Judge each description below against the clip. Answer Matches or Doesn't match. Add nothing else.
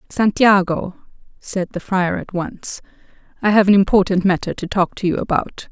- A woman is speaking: Matches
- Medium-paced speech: Matches